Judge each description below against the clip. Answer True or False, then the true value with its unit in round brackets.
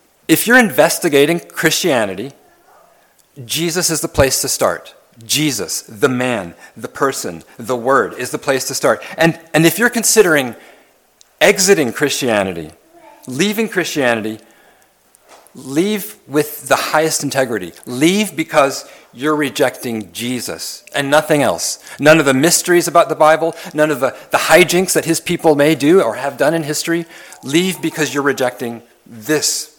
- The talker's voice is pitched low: False (155 Hz)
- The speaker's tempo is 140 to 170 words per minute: True (145 wpm)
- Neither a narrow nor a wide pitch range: True (4.0 semitones)